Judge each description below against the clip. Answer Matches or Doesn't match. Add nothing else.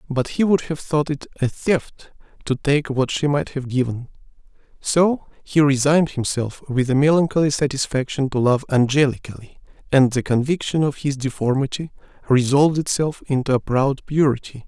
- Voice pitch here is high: Doesn't match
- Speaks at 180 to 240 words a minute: Doesn't match